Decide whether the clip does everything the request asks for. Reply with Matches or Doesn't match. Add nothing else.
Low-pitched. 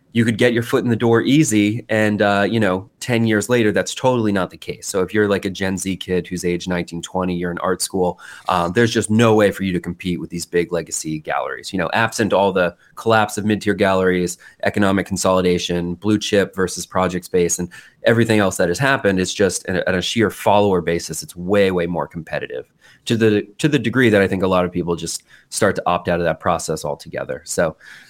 Matches